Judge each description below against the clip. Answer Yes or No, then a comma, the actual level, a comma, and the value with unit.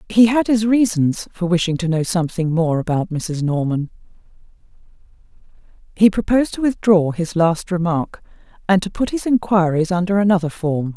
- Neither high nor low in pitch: Yes, medium, 180 Hz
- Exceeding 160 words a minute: No, average, 155 wpm